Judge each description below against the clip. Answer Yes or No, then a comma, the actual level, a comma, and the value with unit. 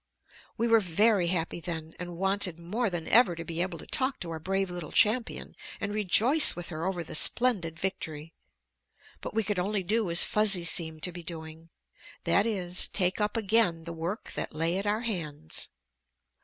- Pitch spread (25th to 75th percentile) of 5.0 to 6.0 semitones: No, average, 4.1 semitones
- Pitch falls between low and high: Yes, medium, 180 Hz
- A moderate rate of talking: Yes, average, 185 wpm